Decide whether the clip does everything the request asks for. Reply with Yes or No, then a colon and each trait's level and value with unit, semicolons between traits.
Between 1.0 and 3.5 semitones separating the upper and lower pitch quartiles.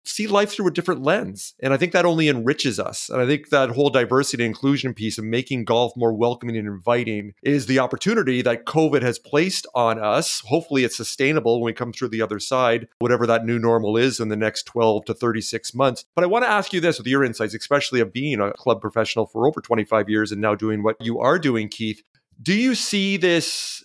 No: average, 4.2 semitones